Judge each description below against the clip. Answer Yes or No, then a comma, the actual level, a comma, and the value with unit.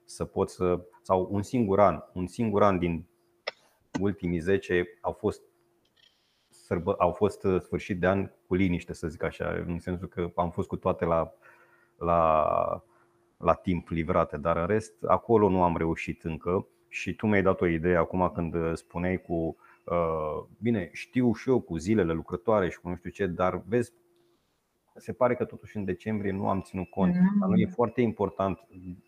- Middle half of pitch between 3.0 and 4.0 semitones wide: Yes, average, 3.7 semitones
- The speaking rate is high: Yes, fast, 175 wpm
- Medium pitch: No, very low, 90 Hz